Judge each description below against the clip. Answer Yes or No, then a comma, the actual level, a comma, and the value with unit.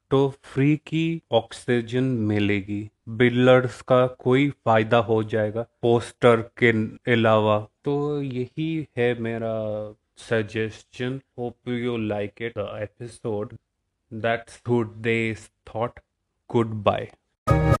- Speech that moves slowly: Yes, slow, 90 wpm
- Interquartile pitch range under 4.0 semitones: Yes, narrow, 2.5 semitones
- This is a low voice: Yes, low, 115 Hz